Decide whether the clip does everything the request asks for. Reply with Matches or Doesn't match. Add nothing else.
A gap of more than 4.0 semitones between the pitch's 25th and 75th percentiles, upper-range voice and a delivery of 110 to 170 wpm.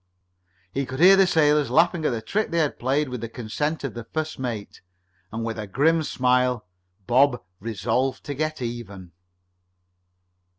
Doesn't match